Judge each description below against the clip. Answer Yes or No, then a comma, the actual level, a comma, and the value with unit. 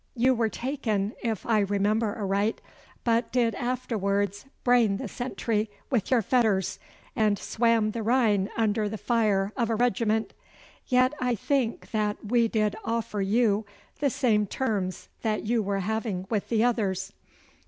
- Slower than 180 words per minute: Yes, average, 150 wpm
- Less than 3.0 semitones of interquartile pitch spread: Yes, narrow, 2.6 semitones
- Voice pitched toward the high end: Yes, high, 220 Hz